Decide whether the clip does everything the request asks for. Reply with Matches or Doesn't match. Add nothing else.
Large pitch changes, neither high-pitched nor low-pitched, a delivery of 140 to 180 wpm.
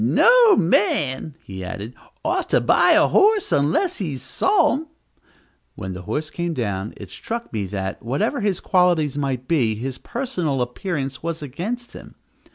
Matches